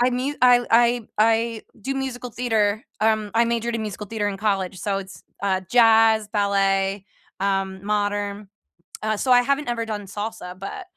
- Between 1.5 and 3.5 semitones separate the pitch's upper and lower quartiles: Yes, average, 2.9 semitones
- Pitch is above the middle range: Yes, high, 215 Hz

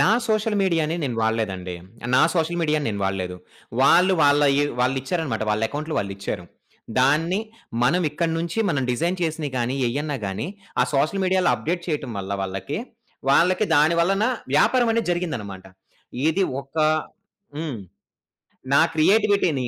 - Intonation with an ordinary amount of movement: No, wide, 6.0 semitones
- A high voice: No, medium, 150 Hz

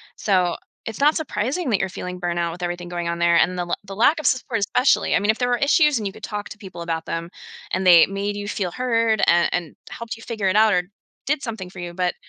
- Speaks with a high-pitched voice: Yes, high, 195 Hz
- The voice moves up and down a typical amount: Yes, average, 4.6 semitones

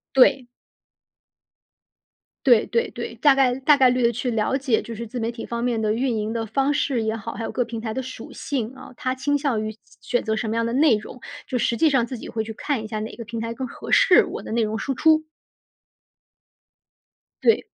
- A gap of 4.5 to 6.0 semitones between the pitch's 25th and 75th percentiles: No, average, 2.9 semitones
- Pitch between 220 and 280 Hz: Yes, high, 235 Hz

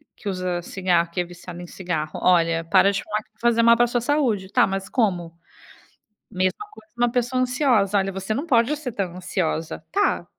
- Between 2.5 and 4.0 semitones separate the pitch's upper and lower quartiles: No, average, 5.3 semitones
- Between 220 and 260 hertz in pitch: No, high, 195 Hz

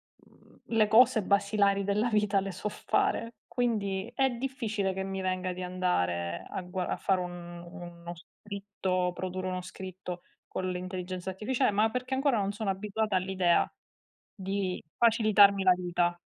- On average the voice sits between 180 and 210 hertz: Yes, high, 190 Hz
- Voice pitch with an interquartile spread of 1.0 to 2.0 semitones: No, narrow, 2.6 semitones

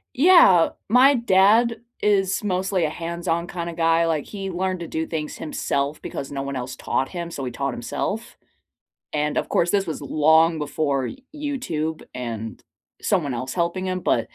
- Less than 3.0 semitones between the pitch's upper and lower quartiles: No, average, 4.4 semitones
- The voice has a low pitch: No, medium, 170 Hz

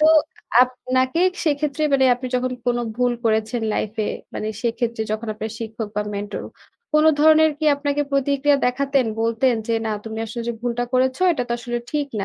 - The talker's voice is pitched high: Yes, very high, 250 Hz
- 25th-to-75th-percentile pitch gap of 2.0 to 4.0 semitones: Yes, average, 3.6 semitones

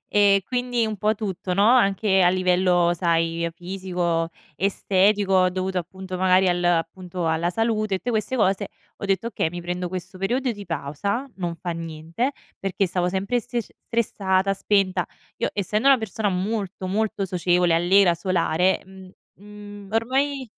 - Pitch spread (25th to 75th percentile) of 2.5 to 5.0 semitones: Yes, average, 2.8 semitones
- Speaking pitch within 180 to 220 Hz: Yes, high, 190 Hz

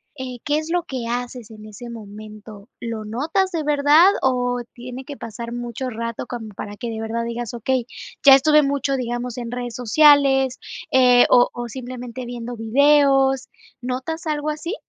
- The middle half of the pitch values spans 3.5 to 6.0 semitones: No, average, 2.9 semitones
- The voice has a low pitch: No, very high, 250 Hz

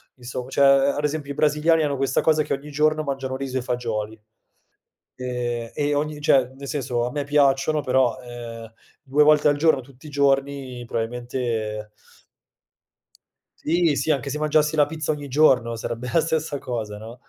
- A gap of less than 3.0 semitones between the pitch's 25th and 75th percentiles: No, average, 3.3 semitones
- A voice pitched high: No, low, 135 Hz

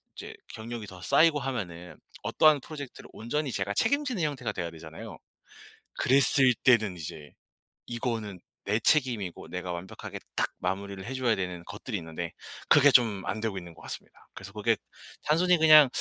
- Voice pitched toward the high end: No, low, 110 Hz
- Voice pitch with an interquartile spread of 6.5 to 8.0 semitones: Yes, wide, 7.1 semitones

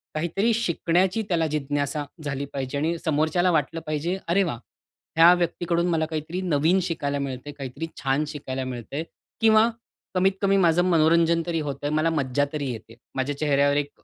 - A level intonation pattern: No, average, 3.3 semitones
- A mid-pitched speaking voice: Yes, medium, 155 Hz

